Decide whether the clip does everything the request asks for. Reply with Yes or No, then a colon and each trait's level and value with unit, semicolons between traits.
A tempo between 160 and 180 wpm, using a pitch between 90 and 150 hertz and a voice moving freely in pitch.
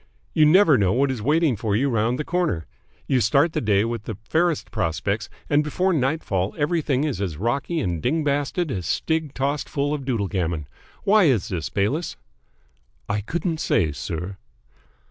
Yes: average, 170 wpm; low, 135 Hz; wide, 7.4 semitones